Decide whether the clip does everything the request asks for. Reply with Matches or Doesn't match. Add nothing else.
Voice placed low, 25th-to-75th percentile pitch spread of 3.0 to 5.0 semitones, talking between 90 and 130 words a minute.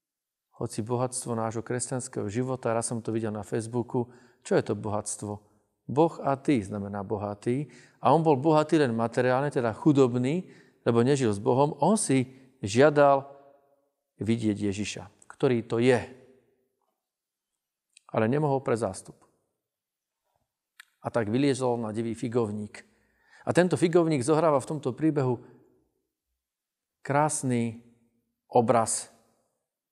Matches